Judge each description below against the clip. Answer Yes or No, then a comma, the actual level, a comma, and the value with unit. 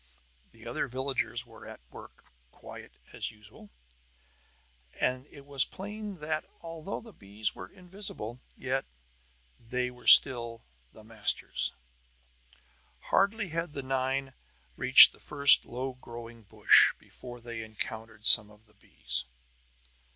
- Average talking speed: No, slow, 125 wpm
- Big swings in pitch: No, average, 4.3 semitones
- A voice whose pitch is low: Yes, low, 125 Hz